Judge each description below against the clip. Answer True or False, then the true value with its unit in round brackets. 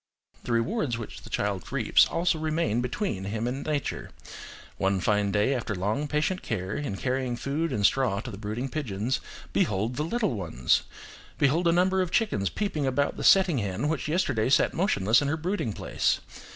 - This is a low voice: True (130 Hz)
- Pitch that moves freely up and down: True (7.1 semitones)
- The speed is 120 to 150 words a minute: False (180 wpm)